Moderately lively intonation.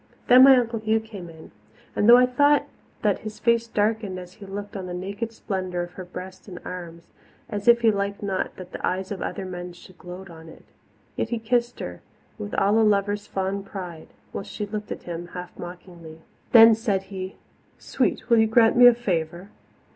Yes: average, 3.7 semitones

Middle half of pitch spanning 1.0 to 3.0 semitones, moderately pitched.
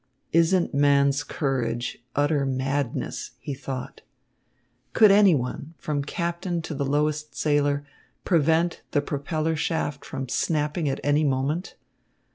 Yes: average, 2.7 semitones; medium, 145 Hz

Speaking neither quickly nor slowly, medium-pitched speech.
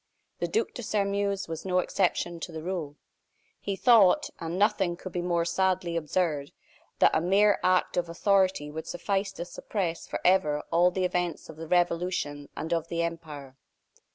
Yes: average, 170 wpm; medium, 175 Hz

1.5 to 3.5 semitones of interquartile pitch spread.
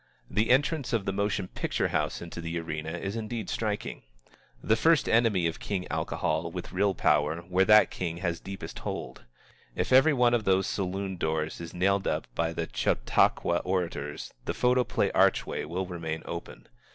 No: average, 4.3 semitones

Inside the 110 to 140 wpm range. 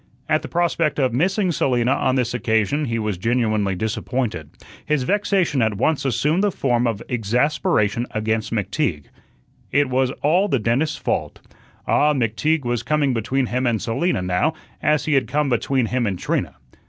No: average, 165 wpm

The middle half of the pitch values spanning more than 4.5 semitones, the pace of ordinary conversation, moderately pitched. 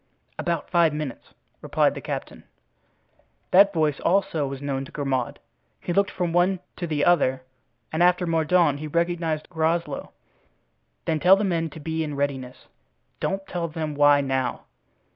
No: average, 3.4 semitones; average, 150 wpm; medium, 160 Hz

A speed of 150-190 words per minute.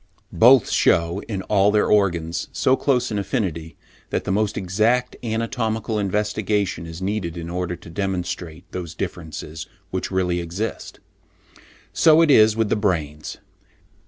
No: average, 140 wpm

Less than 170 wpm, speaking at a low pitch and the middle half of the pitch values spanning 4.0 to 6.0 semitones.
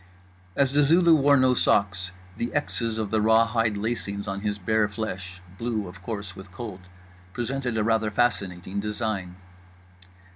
No: average, 150 wpm; low, 110 Hz; average, 3.2 semitones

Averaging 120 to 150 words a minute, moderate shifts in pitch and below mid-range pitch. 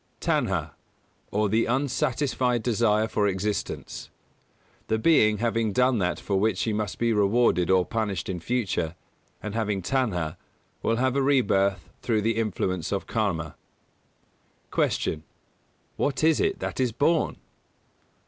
Yes: average, 140 wpm; average, 4.0 semitones; low, 110 Hz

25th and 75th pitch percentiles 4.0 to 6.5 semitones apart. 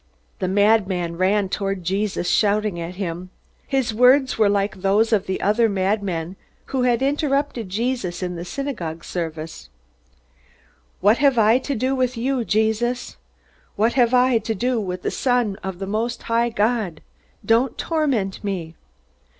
Yes: average, 4.5 semitones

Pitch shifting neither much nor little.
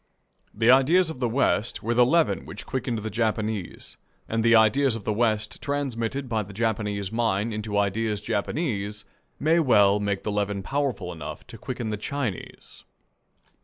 Yes: average, 3.5 semitones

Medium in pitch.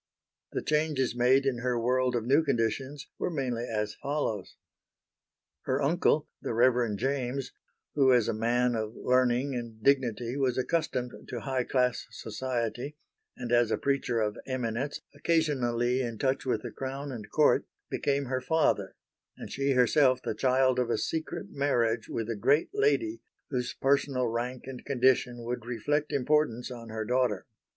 No: low, 125 Hz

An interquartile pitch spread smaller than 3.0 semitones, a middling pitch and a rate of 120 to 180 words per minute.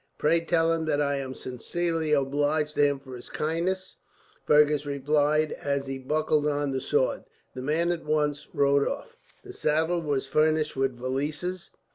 Yes: narrow, 2.5 semitones; medium, 150 Hz; average, 165 wpm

